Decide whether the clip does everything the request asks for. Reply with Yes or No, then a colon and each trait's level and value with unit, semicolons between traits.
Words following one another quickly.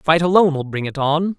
Yes: fast, 260 wpm